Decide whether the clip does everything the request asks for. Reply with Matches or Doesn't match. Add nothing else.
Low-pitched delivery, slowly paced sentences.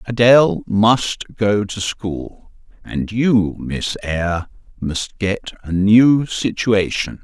Matches